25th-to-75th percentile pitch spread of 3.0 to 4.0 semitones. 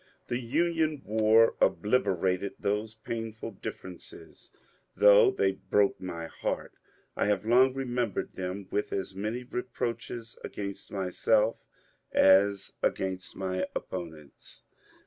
Yes: average, 3.4 semitones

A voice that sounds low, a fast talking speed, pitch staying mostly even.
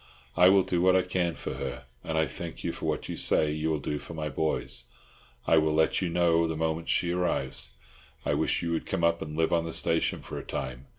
Yes: very low, 80 Hz; fast, 245 wpm; narrow, 1.9 semitones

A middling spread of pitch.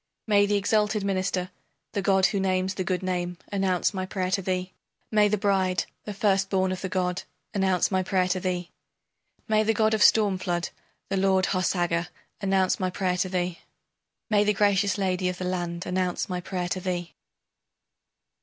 No: narrow, 1.6 semitones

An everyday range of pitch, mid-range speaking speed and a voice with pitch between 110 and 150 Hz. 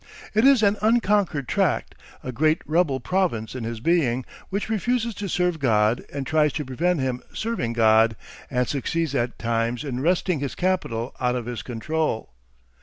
No: wide, 7.0 semitones; average, 170 wpm; medium, 140 Hz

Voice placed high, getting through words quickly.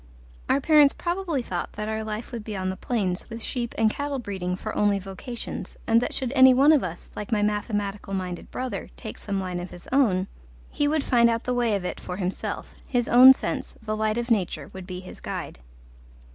Yes: high, 220 Hz; fast, 215 wpm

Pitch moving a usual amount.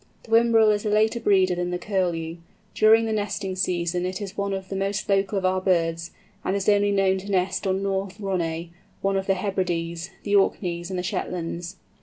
No: narrow, 2.2 semitones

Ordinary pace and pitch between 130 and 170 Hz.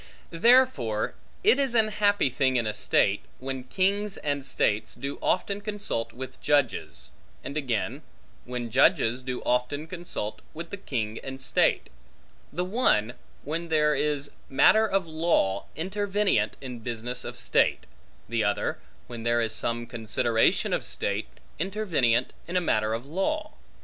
Yes: average, 145 wpm; medium, 140 Hz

